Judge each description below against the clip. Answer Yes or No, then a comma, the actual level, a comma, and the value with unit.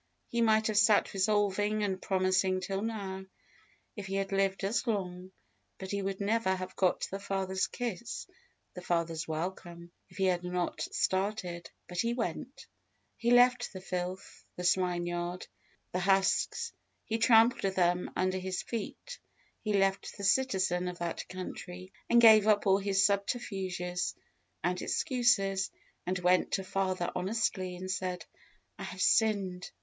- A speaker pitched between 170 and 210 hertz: Yes, high, 190 Hz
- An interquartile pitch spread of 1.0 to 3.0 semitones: Yes, narrow, 2.4 semitones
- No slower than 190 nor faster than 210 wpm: No, average, 155 wpm